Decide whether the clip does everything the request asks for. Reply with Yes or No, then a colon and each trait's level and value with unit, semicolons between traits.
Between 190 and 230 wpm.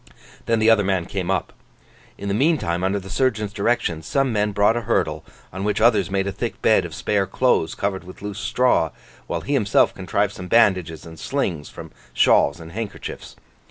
Yes: average, 195 wpm